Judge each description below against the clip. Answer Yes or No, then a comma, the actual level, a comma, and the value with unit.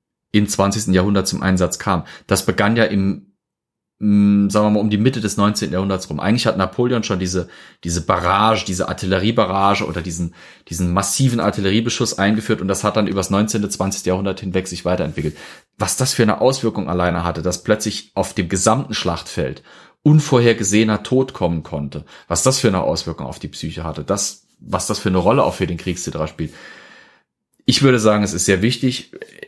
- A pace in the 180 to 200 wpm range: Yes, average, 185 wpm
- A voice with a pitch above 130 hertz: No, low, 100 Hz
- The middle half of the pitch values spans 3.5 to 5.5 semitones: No, average, 2.9 semitones